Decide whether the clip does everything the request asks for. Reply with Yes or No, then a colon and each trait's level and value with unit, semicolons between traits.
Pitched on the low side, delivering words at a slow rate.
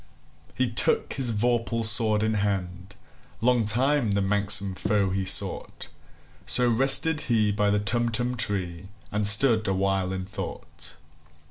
Yes: low, 105 Hz; slow, 120 wpm